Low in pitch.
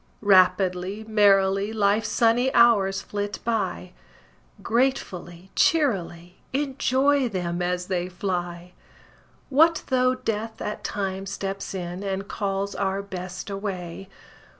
No: high, 195 Hz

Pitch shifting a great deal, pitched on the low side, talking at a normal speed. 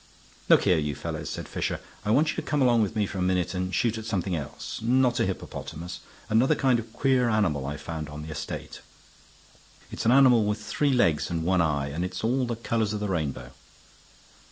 No: wide, 6.3 semitones; low, 105 Hz; fast, 215 wpm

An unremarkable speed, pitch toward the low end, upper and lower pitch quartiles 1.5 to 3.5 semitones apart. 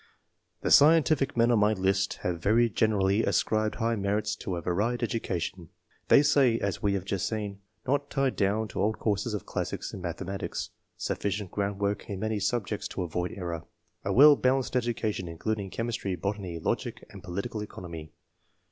Yes: average, 185 wpm; low, 105 Hz; average, 3.2 semitones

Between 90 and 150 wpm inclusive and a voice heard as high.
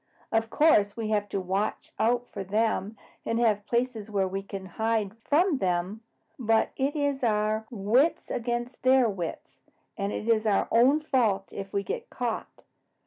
No: average, 165 wpm; high, 220 Hz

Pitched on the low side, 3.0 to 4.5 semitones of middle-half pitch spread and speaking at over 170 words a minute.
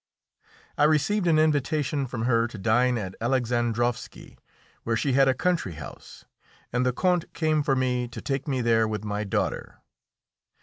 No: low, 125 Hz; average, 4.1 semitones; average, 165 wpm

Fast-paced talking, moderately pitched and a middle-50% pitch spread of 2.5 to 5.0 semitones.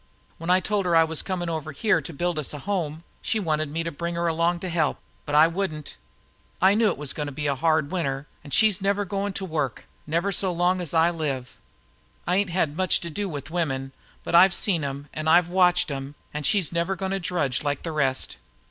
Yes: fast, 235 wpm; medium, 165 Hz; average, 3.7 semitones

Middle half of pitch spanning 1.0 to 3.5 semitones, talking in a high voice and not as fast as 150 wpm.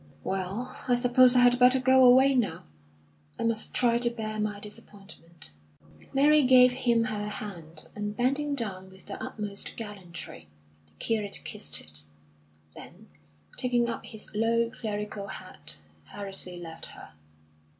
No: average, 3.9 semitones; high, 220 Hz; average, 140 wpm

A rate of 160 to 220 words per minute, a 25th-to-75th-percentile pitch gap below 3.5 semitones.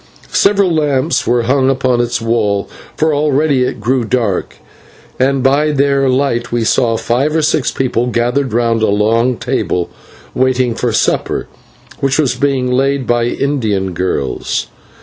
No: average, 150 wpm; average, 3.0 semitones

